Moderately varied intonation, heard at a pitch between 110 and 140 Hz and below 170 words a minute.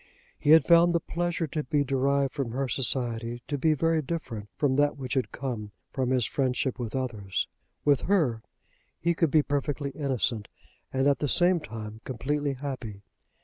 No: average, 3.5 semitones; low, 135 Hz; average, 175 wpm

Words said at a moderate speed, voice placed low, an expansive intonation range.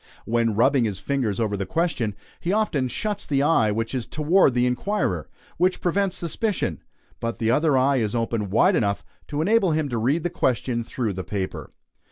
Yes: average, 190 wpm; low, 125 Hz; wide, 6.6 semitones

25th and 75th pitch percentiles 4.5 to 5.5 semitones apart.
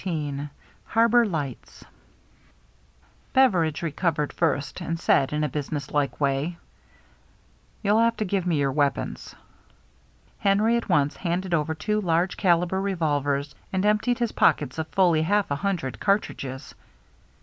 Yes: average, 5.2 semitones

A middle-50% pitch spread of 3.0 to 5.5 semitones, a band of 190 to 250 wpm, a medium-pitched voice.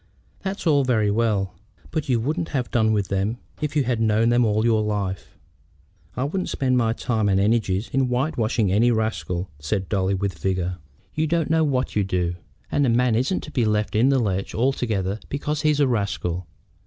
No: average, 4.8 semitones; average, 200 wpm; low, 115 Hz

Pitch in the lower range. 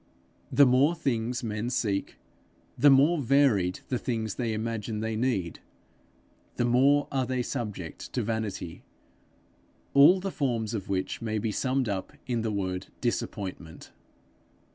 Yes: low, 115 Hz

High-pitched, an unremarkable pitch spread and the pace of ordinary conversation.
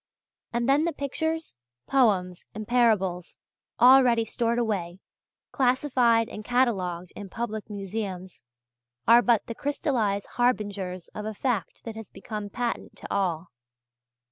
No: high, 225 Hz; average, 3.9 semitones; slow, 125 wpm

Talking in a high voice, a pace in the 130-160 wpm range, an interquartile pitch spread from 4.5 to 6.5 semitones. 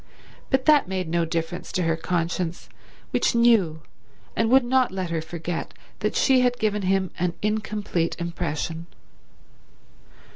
No: medium, 180 Hz; average, 140 wpm; average, 4.8 semitones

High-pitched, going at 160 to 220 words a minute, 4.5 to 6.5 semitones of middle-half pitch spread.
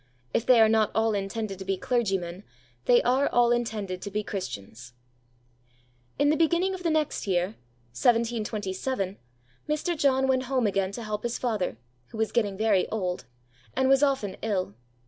Yes: high, 220 Hz; average, 165 wpm; average, 5.0 semitones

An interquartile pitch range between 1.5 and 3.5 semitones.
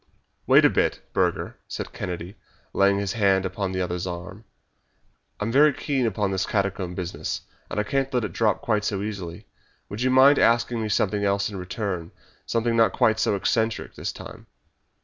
Yes: average, 3.2 semitones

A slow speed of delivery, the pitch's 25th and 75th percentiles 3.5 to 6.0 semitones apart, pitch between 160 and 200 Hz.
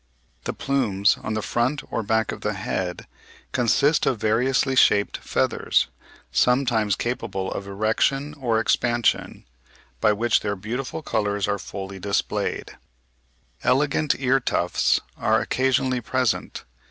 No: slow, 130 wpm; average, 4.1 semitones; low, 115 Hz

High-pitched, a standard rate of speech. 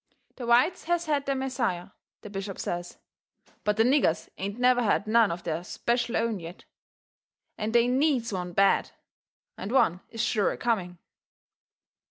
Yes: high, 225 Hz; average, 160 wpm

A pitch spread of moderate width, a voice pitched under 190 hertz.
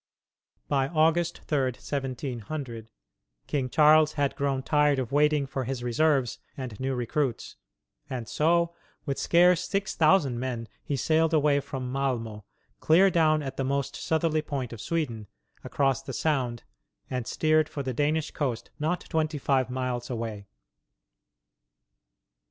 Yes: average, 3.5 semitones; medium, 140 Hz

